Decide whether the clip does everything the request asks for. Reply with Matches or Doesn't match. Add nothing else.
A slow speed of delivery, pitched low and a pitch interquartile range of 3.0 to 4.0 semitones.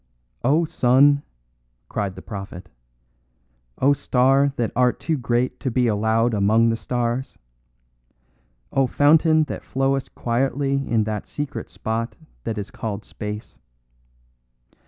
Matches